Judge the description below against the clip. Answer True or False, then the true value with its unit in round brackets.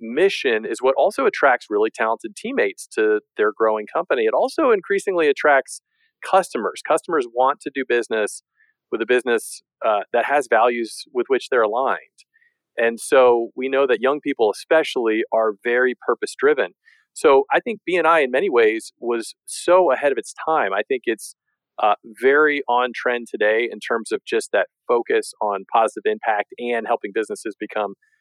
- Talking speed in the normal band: True (170 wpm)